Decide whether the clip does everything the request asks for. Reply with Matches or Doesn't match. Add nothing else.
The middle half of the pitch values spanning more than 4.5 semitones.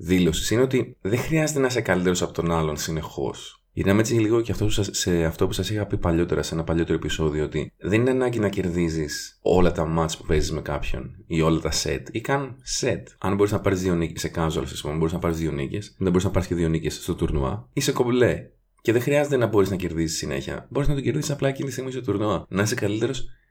Matches